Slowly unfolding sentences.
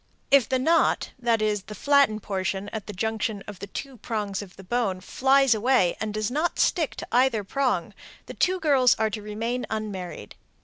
No: average, 190 wpm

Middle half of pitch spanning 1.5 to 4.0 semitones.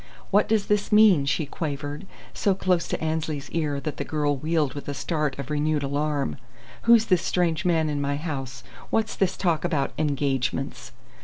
Yes: average, 3.7 semitones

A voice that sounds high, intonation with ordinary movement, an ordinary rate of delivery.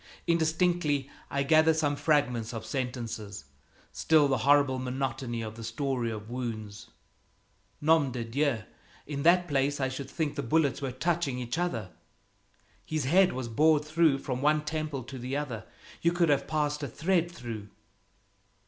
No: medium, 140 Hz; average, 4.2 semitones; average, 155 wpm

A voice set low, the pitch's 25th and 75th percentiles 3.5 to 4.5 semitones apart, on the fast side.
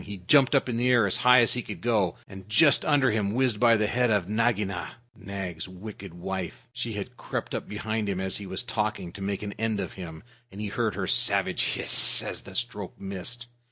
Yes: low, 105 Hz; average, 3.8 semitones; fast, 220 wpm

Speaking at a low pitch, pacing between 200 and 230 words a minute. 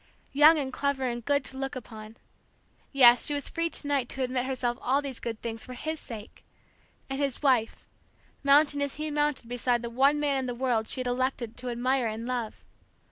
No: very high, 260 Hz; fast, 205 wpm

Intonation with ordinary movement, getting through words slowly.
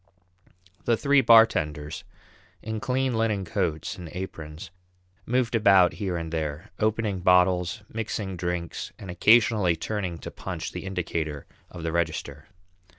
Yes: average, 4.8 semitones; slow, 130 wpm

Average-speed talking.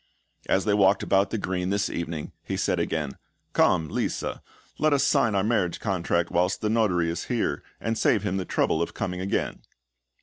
Yes: average, 195 wpm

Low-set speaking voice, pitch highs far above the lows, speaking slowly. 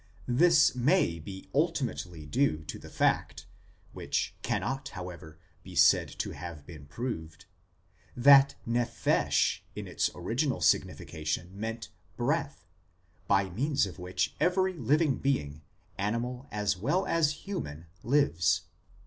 Yes: low, 115 Hz; wide, 8.5 semitones; slow, 125 wpm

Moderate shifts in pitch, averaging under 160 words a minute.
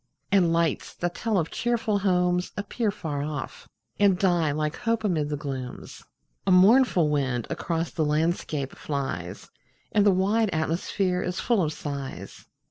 Yes: average, 4.9 semitones; average, 150 wpm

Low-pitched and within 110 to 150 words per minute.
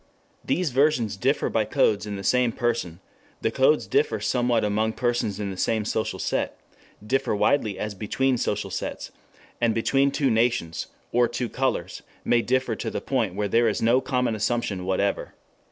No: low, 115 Hz; average, 170 wpm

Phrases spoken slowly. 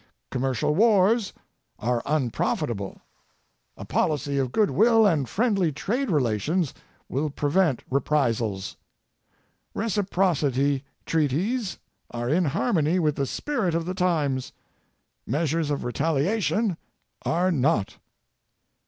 Yes: slow, 100 wpm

